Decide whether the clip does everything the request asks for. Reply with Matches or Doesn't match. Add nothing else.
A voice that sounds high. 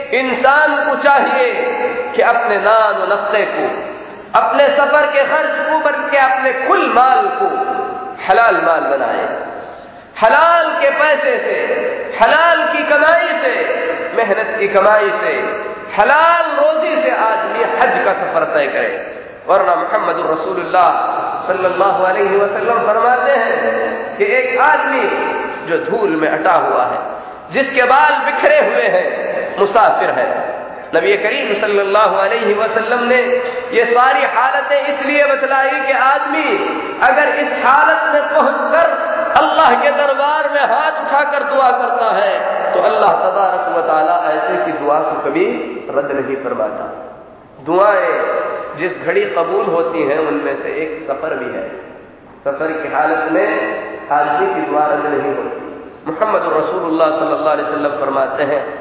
Matches